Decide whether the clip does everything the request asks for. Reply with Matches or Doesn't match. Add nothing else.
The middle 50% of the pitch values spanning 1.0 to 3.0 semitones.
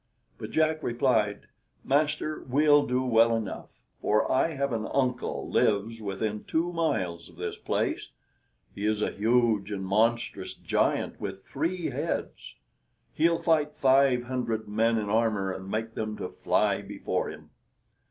Doesn't match